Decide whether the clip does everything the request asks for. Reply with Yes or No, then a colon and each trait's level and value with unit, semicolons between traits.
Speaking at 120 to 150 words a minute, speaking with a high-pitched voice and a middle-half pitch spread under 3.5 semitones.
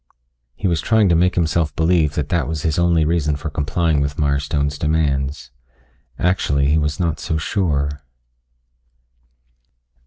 No: average, 145 wpm; very low, 80 Hz; average, 2.8 semitones